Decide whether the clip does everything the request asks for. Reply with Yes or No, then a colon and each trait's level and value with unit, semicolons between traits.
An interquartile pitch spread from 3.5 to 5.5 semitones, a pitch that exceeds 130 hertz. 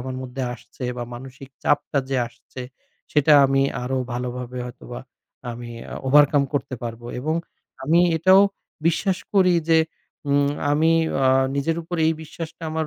Yes: average, 4.2 semitones; medium, 140 Hz